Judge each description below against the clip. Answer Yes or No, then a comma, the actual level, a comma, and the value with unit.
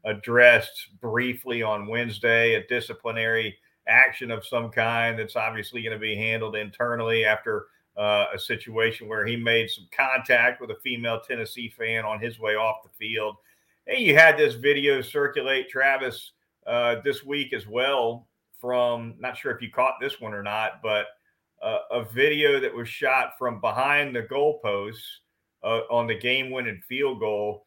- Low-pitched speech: Yes, low, 115 Hz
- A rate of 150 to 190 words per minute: Yes, average, 165 wpm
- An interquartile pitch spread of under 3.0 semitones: Yes, narrow, 2.6 semitones